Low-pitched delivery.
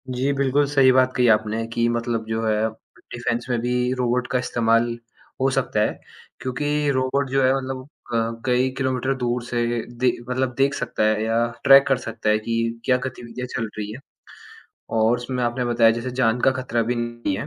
Yes: low, 125 Hz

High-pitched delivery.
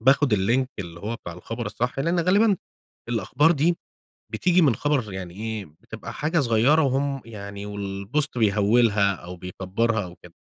No: low, 115 Hz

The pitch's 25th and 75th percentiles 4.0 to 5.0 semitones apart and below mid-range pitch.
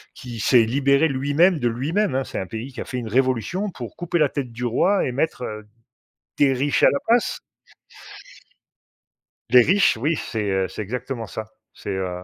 Yes: average, 4.3 semitones; low, 130 Hz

